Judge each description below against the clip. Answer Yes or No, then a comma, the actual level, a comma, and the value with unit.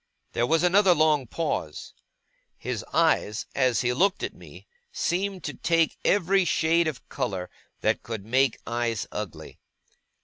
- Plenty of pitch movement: Yes, wide, 6.6 semitones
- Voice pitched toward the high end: No, medium, 150 Hz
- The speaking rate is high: No, average, 140 wpm